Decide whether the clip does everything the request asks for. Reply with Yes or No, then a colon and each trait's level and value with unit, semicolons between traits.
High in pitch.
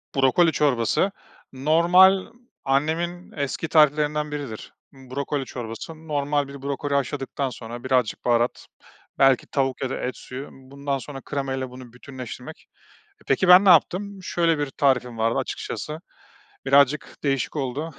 No: medium, 140 Hz